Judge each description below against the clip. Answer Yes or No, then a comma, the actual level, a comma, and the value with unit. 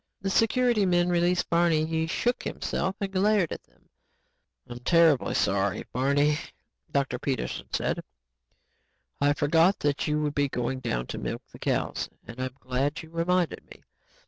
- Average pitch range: Yes, average, 4.7 semitones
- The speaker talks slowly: No, average, 155 wpm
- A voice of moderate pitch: Yes, medium, 160 Hz